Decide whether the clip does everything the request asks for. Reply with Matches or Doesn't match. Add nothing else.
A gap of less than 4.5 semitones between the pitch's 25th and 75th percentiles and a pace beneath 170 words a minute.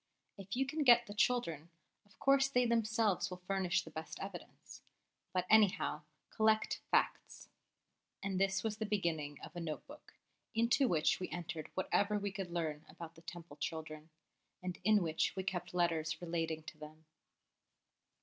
Doesn't match